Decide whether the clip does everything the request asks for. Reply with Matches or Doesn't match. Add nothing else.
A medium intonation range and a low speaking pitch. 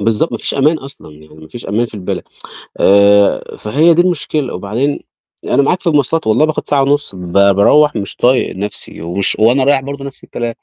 Doesn't match